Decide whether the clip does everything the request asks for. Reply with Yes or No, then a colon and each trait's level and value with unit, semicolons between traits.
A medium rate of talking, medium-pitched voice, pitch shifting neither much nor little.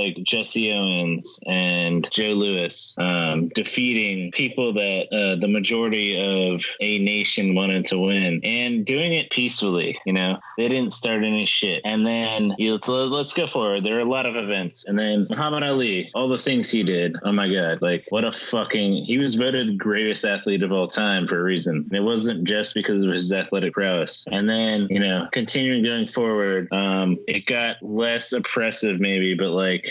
No: average, 185 wpm; low, 100 Hz; average, 3.3 semitones